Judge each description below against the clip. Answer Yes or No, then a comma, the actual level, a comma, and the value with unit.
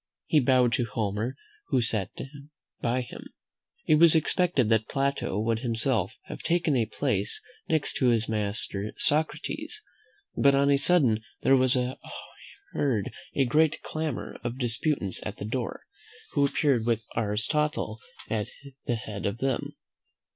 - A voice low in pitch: Yes, low, 125 Hz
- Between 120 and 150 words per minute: Yes, average, 145 wpm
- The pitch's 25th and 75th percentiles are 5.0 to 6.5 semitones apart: No, average, 4.3 semitones